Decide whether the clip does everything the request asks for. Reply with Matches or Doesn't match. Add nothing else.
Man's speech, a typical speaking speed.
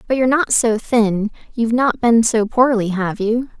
Doesn't match